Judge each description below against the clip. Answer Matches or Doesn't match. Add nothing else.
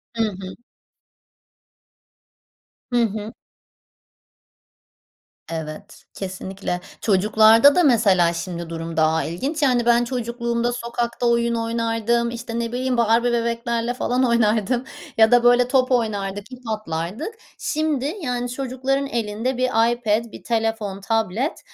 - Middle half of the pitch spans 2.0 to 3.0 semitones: Matches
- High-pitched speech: Matches